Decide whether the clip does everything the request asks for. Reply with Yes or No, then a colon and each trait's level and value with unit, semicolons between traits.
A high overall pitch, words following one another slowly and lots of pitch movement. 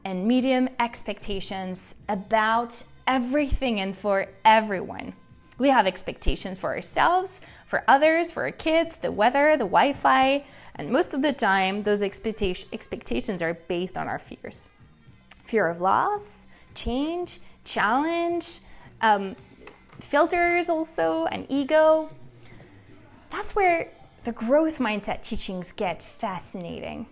Yes: high, 240 Hz; slow, 115 wpm; wide, 7.6 semitones